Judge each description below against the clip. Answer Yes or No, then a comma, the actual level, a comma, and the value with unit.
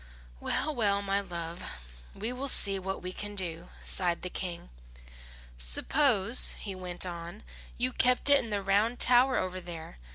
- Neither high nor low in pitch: No, high, 195 Hz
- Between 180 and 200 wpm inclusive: No, average, 160 wpm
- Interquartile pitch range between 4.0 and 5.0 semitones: Yes, average, 4.7 semitones